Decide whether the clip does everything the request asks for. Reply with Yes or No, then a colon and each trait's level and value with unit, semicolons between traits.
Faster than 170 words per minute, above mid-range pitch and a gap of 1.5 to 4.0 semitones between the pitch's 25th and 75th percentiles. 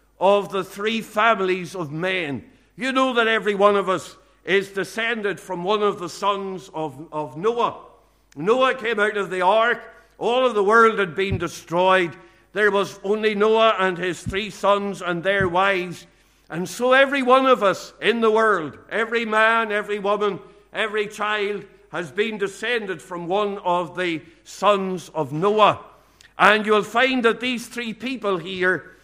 No: average, 165 wpm; high, 200 Hz; average, 3.1 semitones